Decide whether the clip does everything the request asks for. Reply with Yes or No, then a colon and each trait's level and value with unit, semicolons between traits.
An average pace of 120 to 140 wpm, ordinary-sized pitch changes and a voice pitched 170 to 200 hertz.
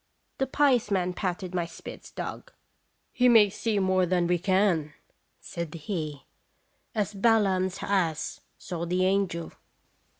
Yes: slow, 135 wpm; average, 3.0 semitones; medium, 185 Hz